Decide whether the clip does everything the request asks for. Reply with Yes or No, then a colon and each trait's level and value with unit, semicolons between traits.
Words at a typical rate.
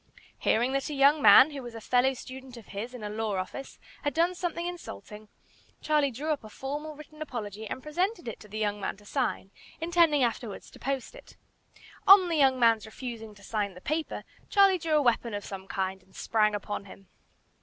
No: fast, 210 wpm